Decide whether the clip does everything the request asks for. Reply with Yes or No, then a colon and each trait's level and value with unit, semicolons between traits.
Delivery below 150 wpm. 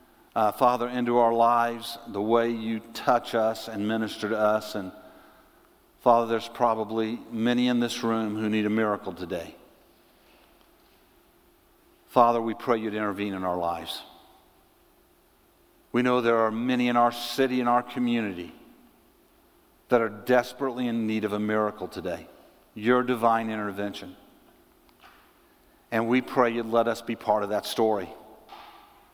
Yes: average, 140 wpm